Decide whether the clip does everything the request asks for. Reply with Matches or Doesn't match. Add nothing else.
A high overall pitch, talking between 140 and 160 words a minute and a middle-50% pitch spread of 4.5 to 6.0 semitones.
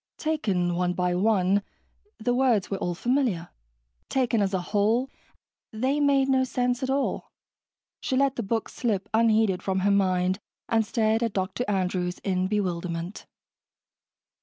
Matches